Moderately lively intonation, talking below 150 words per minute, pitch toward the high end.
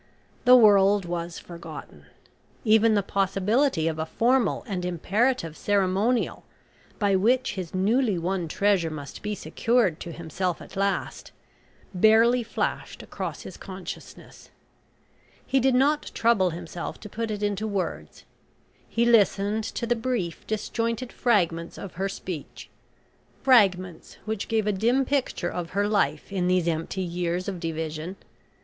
Yes: average, 4.4 semitones; average, 140 wpm; high, 200 Hz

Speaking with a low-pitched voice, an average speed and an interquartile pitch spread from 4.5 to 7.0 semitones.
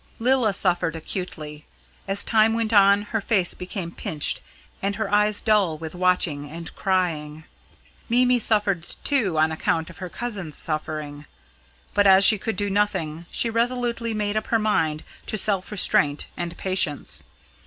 No: high, 195 Hz; average, 155 wpm; average, 4.9 semitones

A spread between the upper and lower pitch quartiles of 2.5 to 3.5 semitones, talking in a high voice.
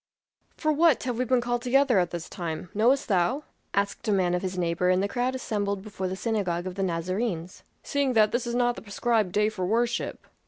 No: average, 4.9 semitones; high, 210 Hz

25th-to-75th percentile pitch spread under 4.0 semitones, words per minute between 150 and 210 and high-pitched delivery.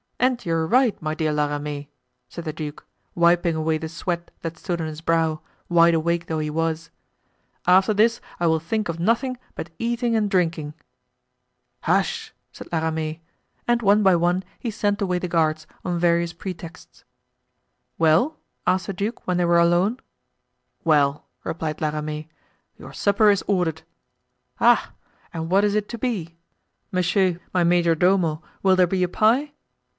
No: average, 3.5 semitones; average, 165 wpm; medium, 170 Hz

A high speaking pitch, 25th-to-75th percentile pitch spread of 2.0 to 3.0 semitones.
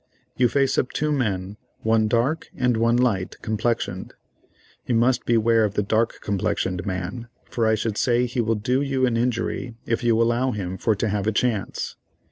No: low, 115 Hz; average, 2.7 semitones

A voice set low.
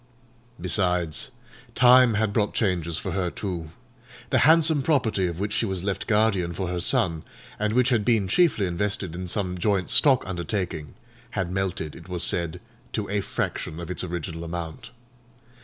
Yes: very low, 95 Hz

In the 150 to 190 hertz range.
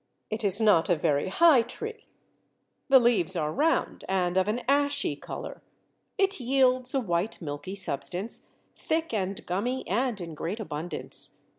No: high, 210 Hz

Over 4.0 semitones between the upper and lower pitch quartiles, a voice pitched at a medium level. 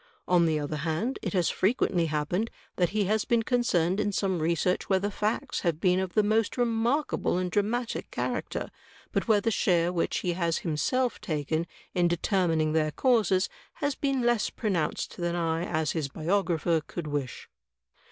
Yes: average, 4.7 semitones; medium, 180 Hz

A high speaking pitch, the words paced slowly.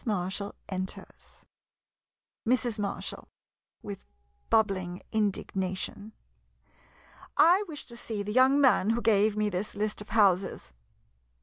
Yes: high, 210 Hz; slow, 115 wpm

